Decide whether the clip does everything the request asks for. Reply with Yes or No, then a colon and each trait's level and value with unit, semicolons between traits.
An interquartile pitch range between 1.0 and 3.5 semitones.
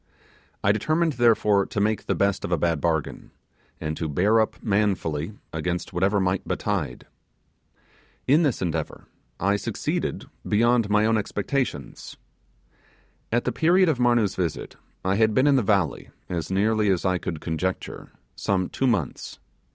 No: average, 4.3 semitones